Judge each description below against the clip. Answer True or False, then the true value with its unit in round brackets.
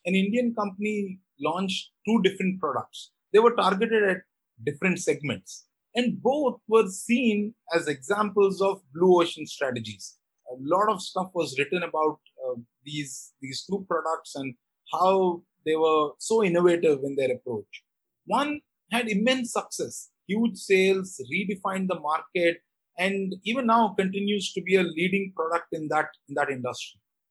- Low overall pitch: False (190 Hz)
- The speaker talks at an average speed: True (145 wpm)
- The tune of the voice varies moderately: True (4.7 semitones)